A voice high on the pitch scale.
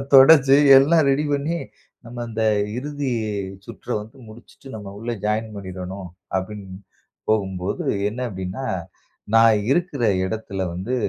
No: low, 110 Hz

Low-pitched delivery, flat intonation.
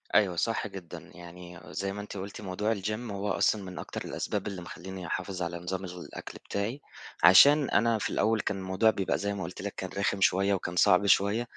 Yes: low, 100 Hz; narrow, 2.2 semitones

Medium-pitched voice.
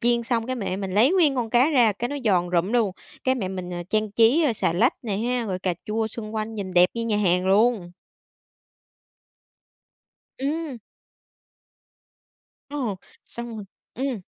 No: high, 225 Hz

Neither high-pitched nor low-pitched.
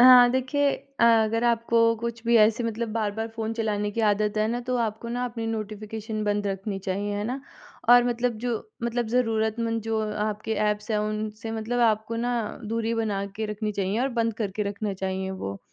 No: high, 220 Hz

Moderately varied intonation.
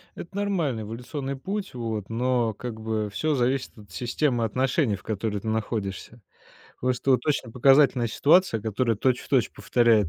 Yes: average, 3.5 semitones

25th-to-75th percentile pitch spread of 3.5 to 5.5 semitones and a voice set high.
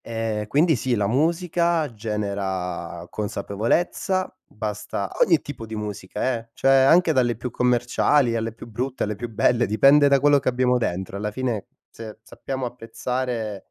No: average, 4.2 semitones; low, 120 Hz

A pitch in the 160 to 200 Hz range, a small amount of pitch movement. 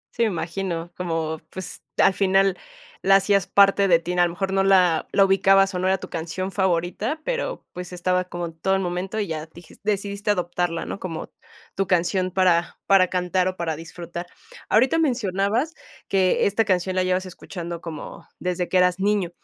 Yes: medium, 185 Hz; narrow, 1.9 semitones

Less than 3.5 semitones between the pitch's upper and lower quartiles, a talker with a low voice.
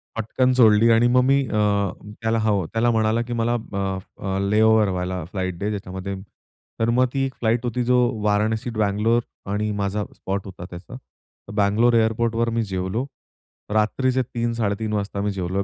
Yes: average, 2.8 semitones; low, 110 Hz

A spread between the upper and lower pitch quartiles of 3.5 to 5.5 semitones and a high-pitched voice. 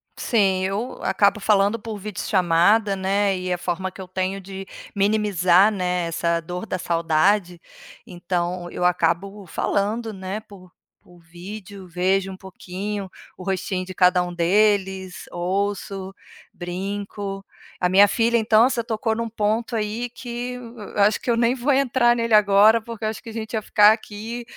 No: average, 2.9 semitones; high, 200 Hz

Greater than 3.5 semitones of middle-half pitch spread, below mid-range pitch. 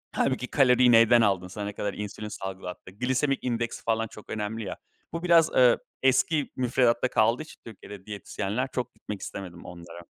Yes: average, 3.9 semitones; low, 115 Hz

